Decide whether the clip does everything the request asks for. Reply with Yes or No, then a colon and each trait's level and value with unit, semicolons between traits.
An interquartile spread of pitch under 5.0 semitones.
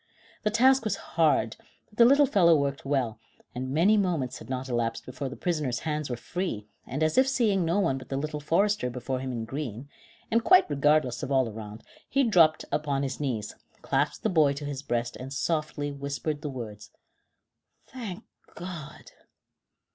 No: wide, 5.4 semitones